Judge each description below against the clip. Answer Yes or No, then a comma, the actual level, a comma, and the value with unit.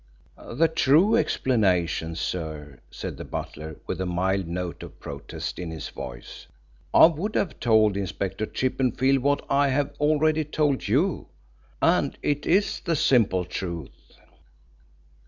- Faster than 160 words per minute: No, slow, 135 wpm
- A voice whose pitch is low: Yes, low, 115 Hz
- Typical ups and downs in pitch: No, wide, 8.8 semitones